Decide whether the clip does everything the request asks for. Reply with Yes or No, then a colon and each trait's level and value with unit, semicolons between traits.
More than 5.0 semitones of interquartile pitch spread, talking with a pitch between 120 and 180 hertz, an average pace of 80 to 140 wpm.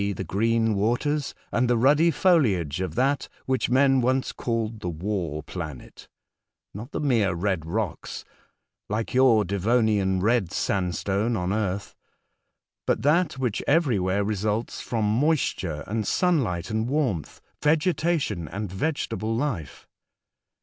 No: wide, 5.6 semitones; low, 110 Hz; slow, 135 wpm